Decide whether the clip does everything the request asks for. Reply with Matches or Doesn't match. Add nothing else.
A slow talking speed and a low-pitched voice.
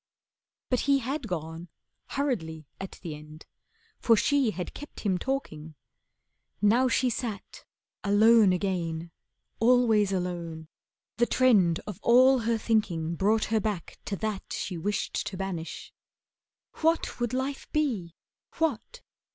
Doesn't match